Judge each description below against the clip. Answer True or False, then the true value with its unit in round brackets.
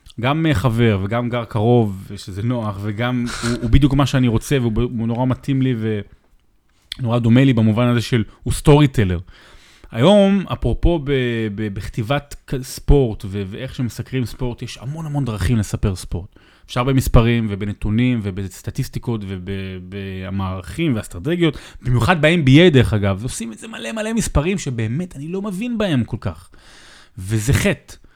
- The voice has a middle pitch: False (120 Hz)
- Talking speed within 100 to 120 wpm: False (145 wpm)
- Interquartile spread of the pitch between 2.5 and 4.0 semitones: False (4.5 semitones)